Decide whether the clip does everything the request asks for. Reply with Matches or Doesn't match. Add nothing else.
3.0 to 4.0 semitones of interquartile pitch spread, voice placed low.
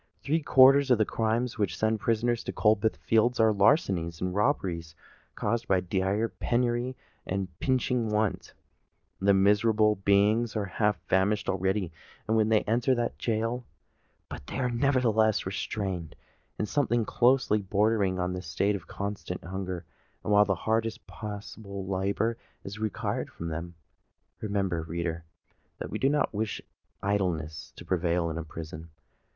Matches